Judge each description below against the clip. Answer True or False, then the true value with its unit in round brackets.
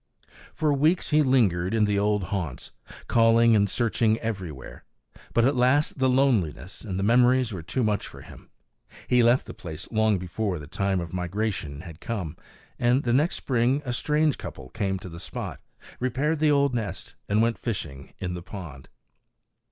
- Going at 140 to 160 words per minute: False (175 wpm)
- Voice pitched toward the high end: False (110 Hz)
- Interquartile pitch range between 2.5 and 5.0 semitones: False (5.5 semitones)